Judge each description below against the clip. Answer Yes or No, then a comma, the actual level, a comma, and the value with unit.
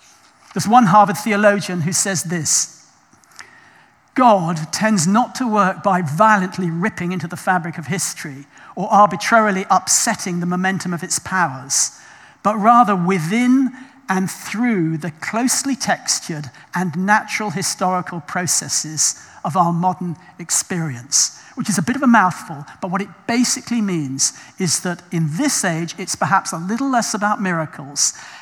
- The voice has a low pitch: No, high, 190 Hz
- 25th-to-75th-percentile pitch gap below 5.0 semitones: Yes, average, 3.9 semitones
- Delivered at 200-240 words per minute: No, average, 145 wpm